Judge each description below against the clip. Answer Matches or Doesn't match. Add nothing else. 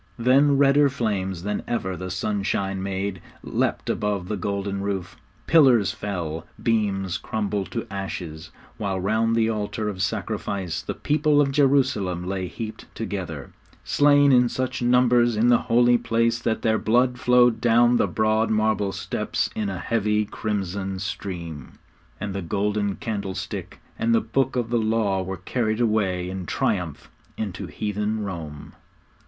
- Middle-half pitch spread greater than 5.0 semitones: Doesn't match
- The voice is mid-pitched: Doesn't match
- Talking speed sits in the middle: Matches